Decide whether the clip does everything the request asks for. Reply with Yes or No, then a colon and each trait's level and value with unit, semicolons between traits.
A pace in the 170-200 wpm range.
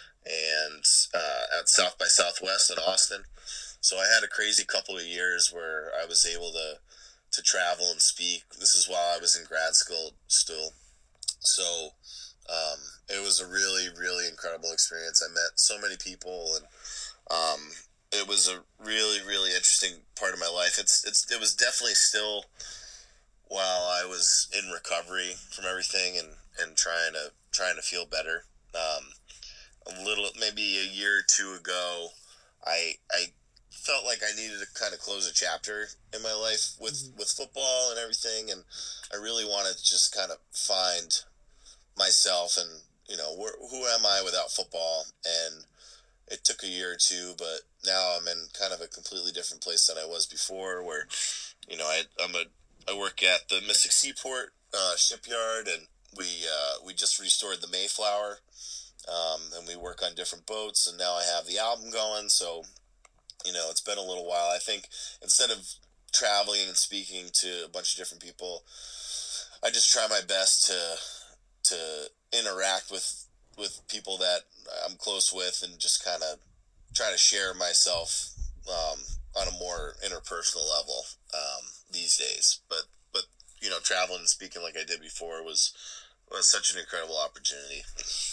Yes: average, 175 wpm